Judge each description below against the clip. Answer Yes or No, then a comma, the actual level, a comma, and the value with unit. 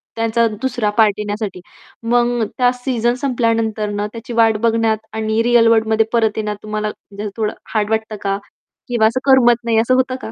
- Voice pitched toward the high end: Yes, high, 225 Hz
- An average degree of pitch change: No, narrow, 1.9 semitones